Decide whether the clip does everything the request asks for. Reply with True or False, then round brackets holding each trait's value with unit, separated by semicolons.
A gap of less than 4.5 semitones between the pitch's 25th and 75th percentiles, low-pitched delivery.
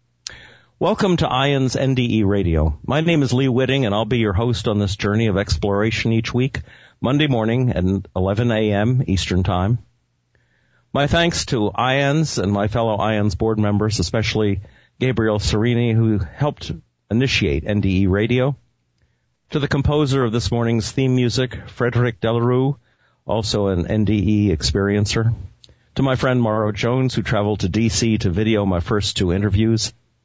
True (3.6 semitones; 110 Hz)